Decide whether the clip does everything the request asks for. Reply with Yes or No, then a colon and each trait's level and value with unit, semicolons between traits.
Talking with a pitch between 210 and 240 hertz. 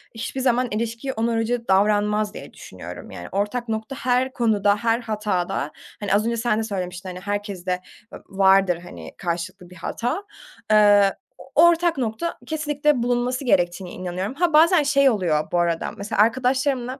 Yes: high, 220 Hz